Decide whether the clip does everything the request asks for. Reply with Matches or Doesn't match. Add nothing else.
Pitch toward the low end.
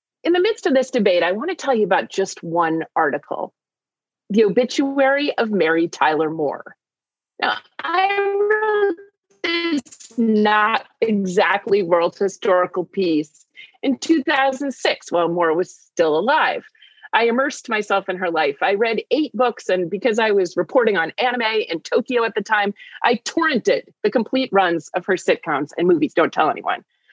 Doesn't match